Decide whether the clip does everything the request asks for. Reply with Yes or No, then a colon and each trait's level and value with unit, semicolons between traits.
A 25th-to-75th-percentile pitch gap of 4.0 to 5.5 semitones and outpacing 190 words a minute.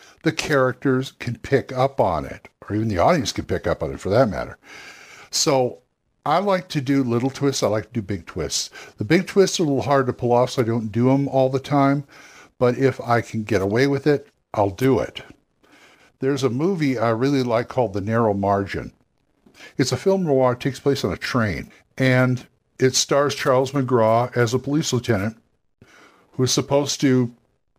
No: average, 2.9 semitones; fast, 205 wpm